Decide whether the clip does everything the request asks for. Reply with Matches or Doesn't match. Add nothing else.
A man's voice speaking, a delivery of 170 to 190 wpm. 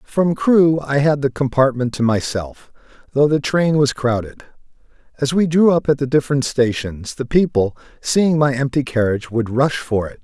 Matches